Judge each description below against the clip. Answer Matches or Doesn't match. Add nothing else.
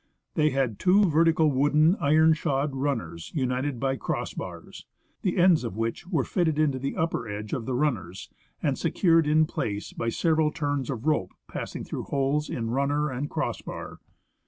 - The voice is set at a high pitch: Doesn't match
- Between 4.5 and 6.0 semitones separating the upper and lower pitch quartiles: Doesn't match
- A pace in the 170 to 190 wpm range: Matches